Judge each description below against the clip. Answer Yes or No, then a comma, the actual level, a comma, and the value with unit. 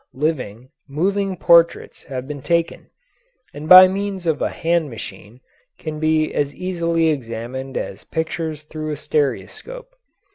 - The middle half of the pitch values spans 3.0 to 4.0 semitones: Yes, average, 3.4 semitones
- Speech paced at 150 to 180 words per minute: No, slow, 135 wpm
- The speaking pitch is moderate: Yes, medium, 155 Hz